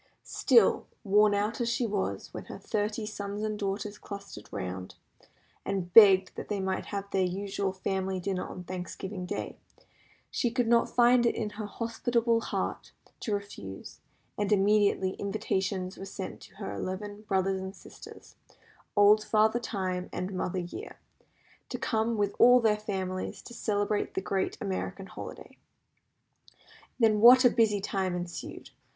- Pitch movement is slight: Yes, narrow, 2.3 semitones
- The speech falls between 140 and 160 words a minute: Yes, average, 150 wpm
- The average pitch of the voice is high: Yes, high, 200 Hz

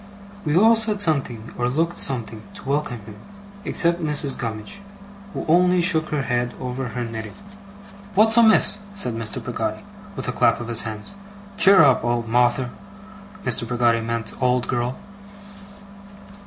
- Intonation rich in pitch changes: Yes, wide, 6.3 semitones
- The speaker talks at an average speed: Yes, average, 150 wpm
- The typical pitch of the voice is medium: No, low, 125 Hz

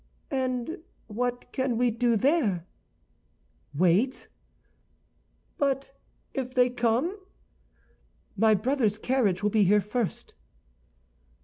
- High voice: Yes, high, 245 Hz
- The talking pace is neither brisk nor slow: No, slow, 95 wpm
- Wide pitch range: No, average, 3.8 semitones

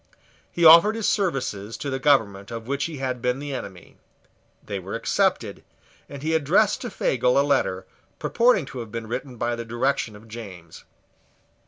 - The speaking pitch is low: Yes, low, 130 Hz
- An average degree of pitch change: No, wide, 5.7 semitones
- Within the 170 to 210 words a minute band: Yes, average, 175 wpm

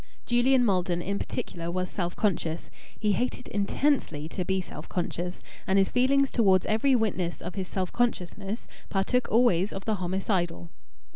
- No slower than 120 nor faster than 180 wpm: Yes, average, 155 wpm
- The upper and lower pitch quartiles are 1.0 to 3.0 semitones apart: No, average, 4.7 semitones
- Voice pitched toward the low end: No, high, 195 Hz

